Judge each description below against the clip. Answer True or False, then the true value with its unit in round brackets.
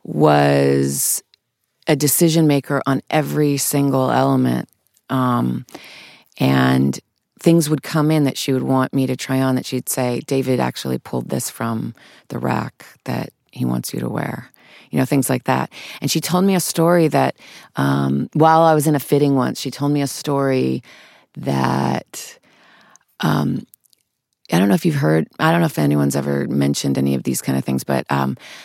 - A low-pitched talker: True (130 Hz)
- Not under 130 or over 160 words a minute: False (180 wpm)